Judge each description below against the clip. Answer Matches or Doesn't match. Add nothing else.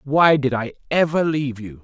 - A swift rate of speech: Doesn't match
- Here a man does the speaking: Matches